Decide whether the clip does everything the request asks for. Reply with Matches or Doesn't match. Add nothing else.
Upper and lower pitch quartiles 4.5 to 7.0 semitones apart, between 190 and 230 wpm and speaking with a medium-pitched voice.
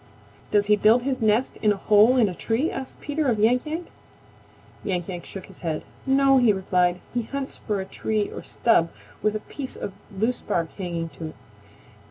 Doesn't match